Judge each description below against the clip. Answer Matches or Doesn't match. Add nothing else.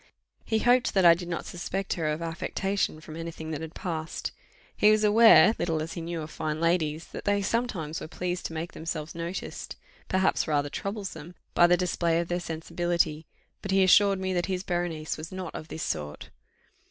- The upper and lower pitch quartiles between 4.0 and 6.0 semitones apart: Doesn't match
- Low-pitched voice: Doesn't match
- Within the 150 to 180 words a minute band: Doesn't match